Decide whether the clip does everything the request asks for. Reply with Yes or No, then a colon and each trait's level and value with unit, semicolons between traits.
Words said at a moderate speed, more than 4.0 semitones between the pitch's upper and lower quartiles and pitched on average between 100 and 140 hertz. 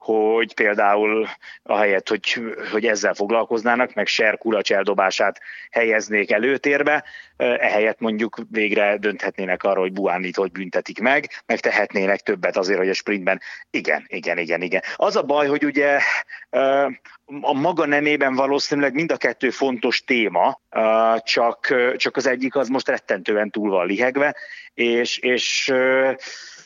Yes: average, 135 wpm; average, 4.7 semitones; low, 115 Hz